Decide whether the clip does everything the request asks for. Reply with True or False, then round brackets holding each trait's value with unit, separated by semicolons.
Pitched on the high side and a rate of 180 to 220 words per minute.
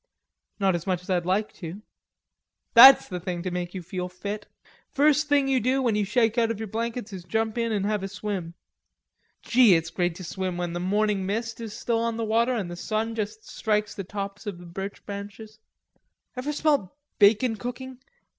True (210 Hz; 200 wpm)